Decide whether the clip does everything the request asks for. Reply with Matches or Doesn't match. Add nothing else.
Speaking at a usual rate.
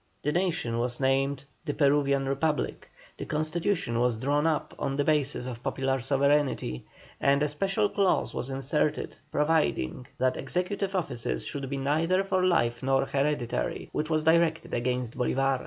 Matches